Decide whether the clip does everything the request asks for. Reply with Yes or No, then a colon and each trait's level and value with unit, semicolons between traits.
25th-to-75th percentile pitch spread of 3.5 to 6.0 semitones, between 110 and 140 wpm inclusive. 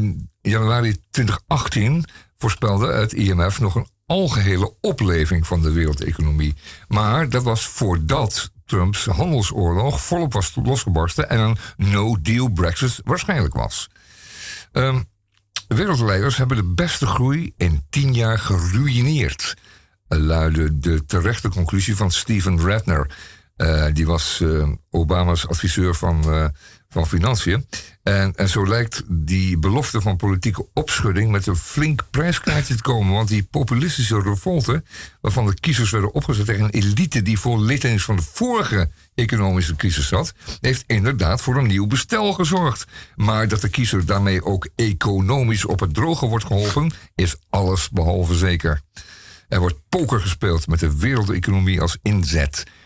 Yes: average, 5.1 semitones; slow, 135 wpm